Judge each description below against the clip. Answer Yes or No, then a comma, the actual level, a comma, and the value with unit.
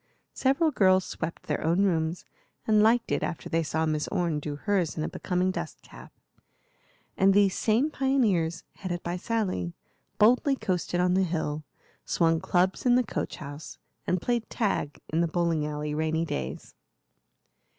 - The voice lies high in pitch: No, medium, 175 Hz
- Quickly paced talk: No, average, 160 wpm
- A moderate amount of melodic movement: Yes, average, 4.5 semitones